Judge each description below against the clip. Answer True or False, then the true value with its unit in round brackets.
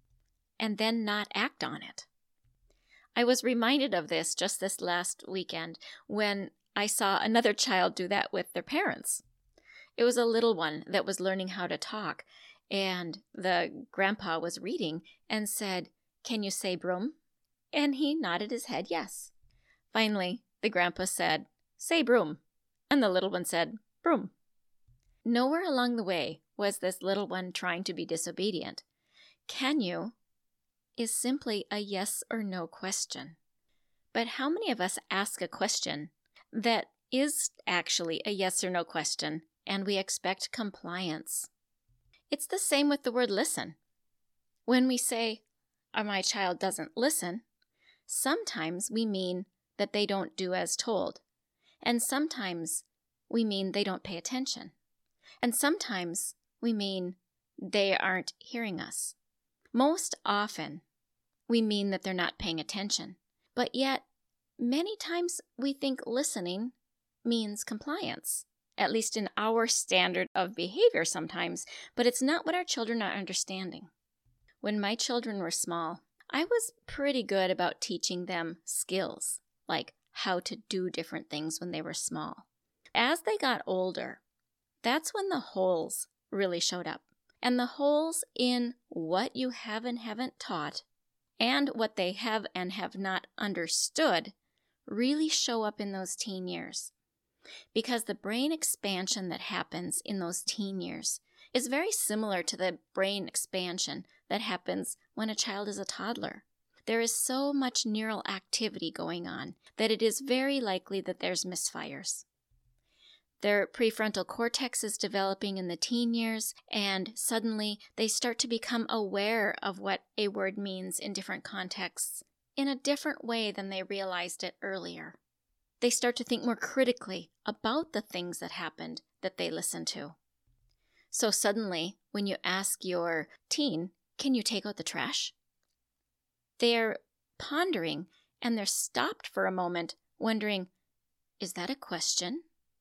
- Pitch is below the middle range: False (205 Hz)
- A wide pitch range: False (4.9 semitones)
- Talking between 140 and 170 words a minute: True (150 wpm)